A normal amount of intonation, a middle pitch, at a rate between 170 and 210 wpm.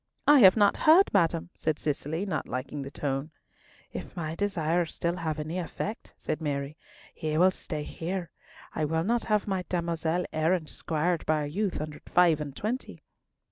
Yes: average, 3.3 semitones; medium, 165 Hz; average, 175 wpm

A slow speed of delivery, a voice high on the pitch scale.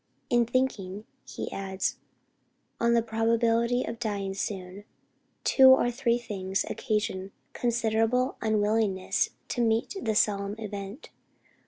Yes: slow, 115 wpm; high, 220 Hz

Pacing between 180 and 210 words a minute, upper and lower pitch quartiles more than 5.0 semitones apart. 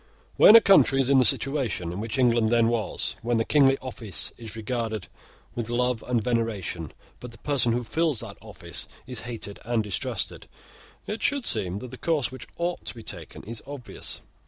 No: average, 190 wpm; average, 3.1 semitones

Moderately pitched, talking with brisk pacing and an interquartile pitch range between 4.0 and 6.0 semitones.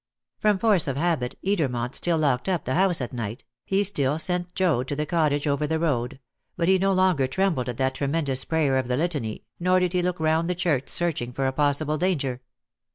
Yes: medium, 155 Hz; fast, 215 wpm; average, 5.1 semitones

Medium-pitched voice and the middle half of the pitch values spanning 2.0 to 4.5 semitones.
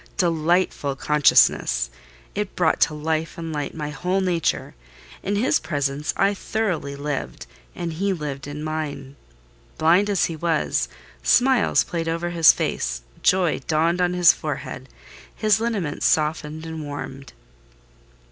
Yes: medium, 160 Hz; average, 3.2 semitones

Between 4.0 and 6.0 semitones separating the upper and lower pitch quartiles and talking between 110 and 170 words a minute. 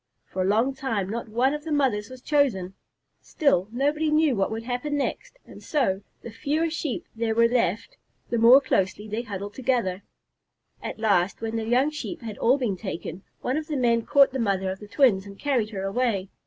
No: average, 5.1 semitones; fast, 205 wpm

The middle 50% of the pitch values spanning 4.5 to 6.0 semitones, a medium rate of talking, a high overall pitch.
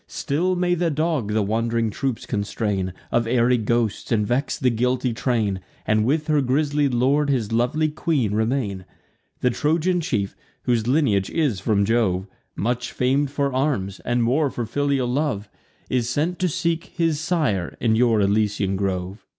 No: average, 5.2 semitones; average, 160 wpm; low, 125 Hz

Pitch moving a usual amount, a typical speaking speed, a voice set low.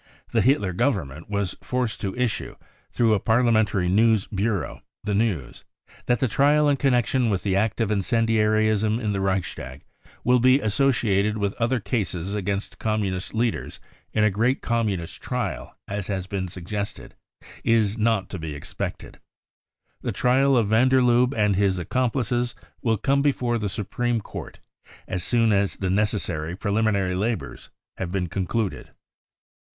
Yes: average, 3.5 semitones; average, 155 wpm; low, 105 Hz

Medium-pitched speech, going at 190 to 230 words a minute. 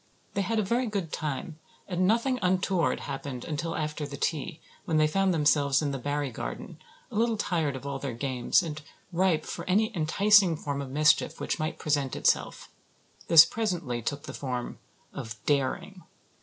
No: medium, 155 Hz; average, 170 wpm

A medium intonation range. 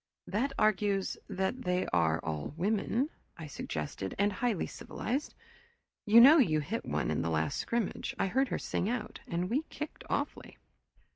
No: wide, 6.8 semitones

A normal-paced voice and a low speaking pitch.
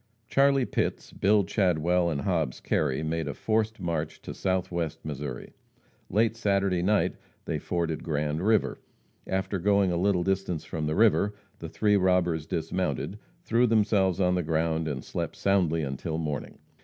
Yes: average, 155 wpm; very low, 90 Hz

